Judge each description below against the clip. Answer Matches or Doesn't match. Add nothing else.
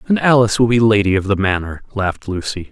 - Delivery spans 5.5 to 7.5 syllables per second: Matches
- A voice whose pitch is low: Matches